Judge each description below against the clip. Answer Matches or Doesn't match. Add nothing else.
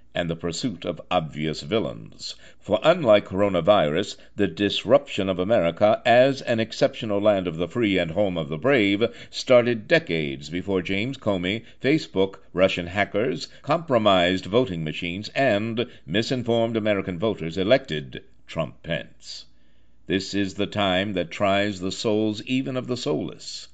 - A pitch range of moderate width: Matches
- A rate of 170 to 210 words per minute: Doesn't match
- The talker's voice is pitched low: Matches